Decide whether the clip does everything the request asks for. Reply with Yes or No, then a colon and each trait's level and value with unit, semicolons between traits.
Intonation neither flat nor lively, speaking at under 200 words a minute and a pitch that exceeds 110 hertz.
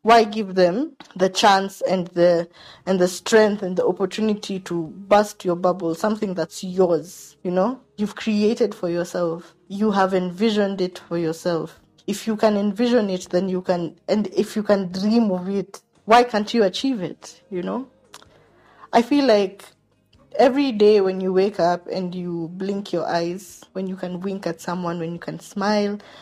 Yes: average, 3.1 semitones; average, 180 wpm; high, 190 Hz